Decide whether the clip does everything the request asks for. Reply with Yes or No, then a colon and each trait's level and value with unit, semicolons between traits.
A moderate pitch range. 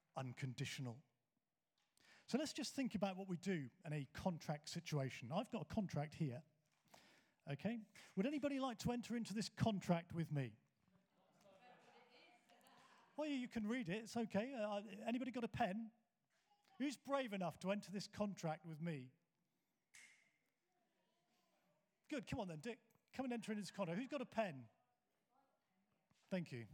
No: wide, 6.9 semitones